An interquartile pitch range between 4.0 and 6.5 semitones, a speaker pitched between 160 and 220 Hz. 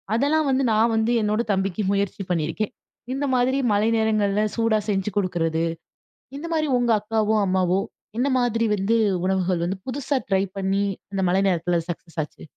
No: average, 3.5 semitones; high, 210 Hz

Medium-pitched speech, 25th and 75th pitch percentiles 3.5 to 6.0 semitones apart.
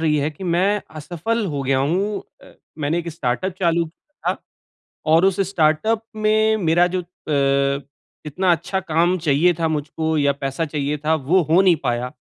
Yes: medium, 165 Hz; average, 3.9 semitones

